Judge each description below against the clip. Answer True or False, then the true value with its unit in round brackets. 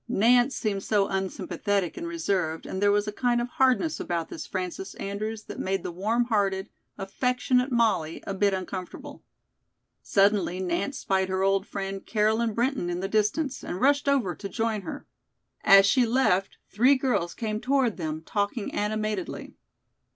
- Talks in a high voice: True (205 Hz)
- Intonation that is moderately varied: True (3.9 semitones)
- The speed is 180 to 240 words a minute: False (160 wpm)